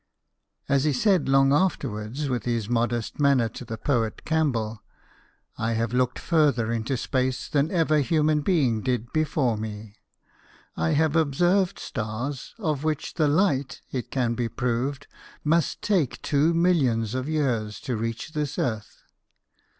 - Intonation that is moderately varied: Yes, average, 4.7 semitones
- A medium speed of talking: Yes, average, 150 wpm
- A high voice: No, low, 130 Hz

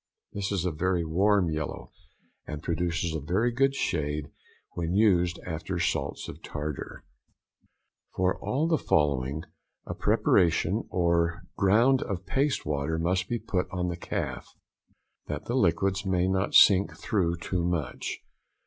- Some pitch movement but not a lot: Yes, average, 3.3 semitones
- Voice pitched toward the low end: Yes, very low, 90 Hz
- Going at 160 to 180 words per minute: No, average, 140 wpm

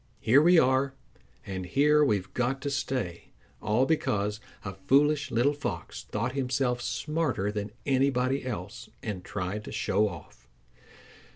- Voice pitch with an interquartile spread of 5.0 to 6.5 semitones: Yes, average, 5.3 semitones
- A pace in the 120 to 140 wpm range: Yes, slow, 135 wpm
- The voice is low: Yes, low, 125 Hz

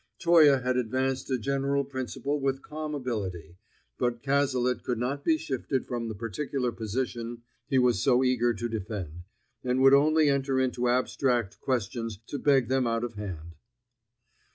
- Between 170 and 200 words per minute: No, average, 155 wpm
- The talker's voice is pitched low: Yes, low, 125 Hz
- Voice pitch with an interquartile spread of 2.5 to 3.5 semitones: Yes, average, 2.9 semitones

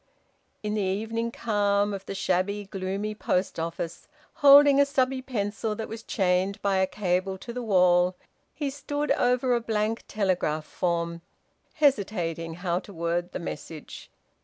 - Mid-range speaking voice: No, high, 200 Hz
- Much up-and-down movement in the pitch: No, average, 4.0 semitones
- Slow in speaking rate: No, average, 150 wpm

